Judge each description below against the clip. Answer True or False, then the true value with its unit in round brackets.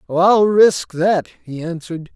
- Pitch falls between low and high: True (175 Hz)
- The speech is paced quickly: False (140 wpm)